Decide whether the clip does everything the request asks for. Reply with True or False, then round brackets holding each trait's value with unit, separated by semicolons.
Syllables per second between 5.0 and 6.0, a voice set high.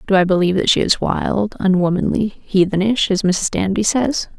True (5.1 syllables/s; 195 Hz)